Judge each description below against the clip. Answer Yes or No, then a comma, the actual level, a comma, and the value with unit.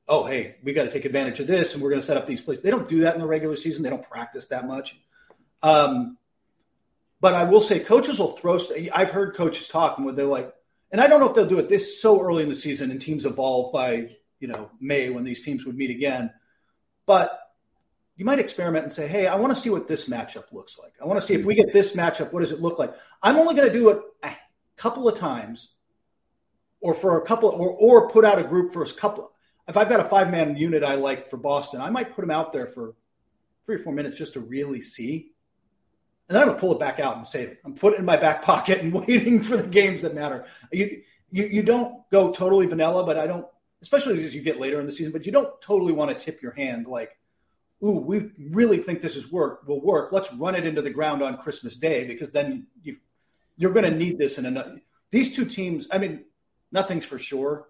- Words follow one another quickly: Yes, fast, 250 wpm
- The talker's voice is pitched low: No, medium, 175 Hz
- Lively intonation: Yes, wide, 6.3 semitones